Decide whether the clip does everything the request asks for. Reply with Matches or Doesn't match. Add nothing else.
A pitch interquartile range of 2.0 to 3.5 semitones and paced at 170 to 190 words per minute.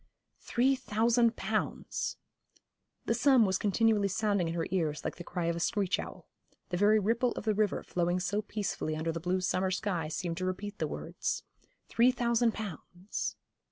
Doesn't match